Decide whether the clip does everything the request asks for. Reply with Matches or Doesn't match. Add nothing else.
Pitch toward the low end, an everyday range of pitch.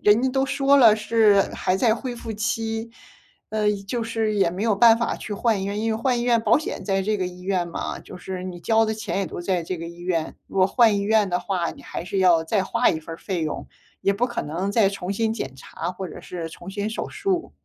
Doesn't match